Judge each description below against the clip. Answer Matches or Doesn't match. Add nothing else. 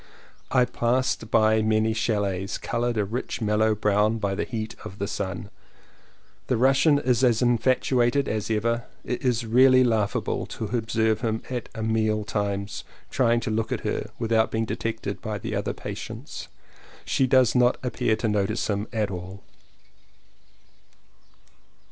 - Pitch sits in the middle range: Doesn't match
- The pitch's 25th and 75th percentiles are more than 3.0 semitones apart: Doesn't match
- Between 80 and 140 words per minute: Doesn't match